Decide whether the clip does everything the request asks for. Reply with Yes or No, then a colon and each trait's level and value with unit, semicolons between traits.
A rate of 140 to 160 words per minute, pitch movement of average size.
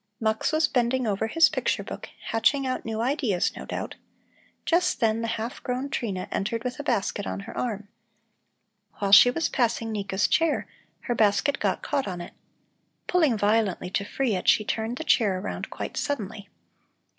No: average, 175 wpm; average, 4.2 semitones